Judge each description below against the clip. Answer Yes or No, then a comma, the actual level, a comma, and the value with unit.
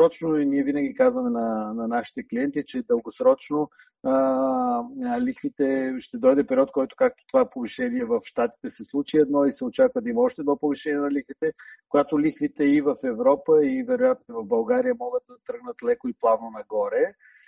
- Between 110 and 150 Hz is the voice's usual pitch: No, high, 240 Hz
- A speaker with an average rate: No, fast, 170 wpm